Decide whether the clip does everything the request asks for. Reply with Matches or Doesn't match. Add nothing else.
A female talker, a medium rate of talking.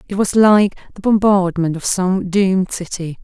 Matches